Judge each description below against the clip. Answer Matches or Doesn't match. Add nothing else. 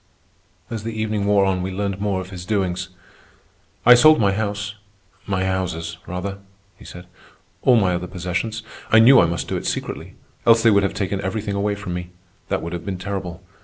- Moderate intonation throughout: Doesn't match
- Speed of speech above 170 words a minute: Matches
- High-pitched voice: Doesn't match